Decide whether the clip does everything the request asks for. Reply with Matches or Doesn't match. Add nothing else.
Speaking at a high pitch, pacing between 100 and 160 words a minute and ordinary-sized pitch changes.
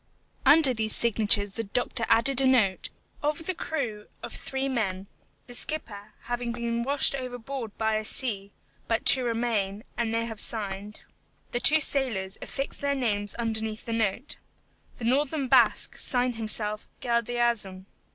Matches